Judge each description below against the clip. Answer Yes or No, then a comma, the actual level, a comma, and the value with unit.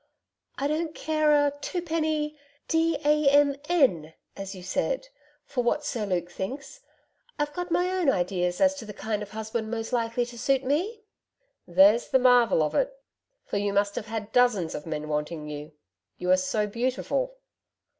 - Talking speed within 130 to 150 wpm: No, average, 175 wpm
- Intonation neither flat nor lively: No, wide, 7.3 semitones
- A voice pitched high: Yes, high, 240 Hz